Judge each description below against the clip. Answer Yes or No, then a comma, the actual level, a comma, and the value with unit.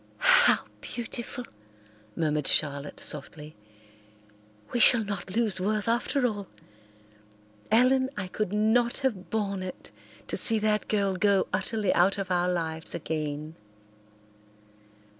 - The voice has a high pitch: Yes, high, 200 Hz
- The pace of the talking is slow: Yes, slow, 120 wpm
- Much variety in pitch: No, average, 4.6 semitones